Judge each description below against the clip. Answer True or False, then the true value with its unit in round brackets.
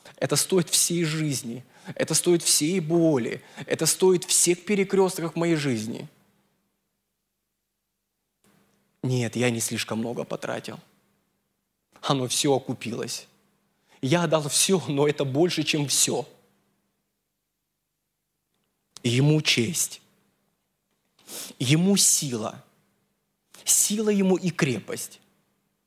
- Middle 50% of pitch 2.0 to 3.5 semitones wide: False (5.1 semitones)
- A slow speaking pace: True (90 wpm)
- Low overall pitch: False (155 Hz)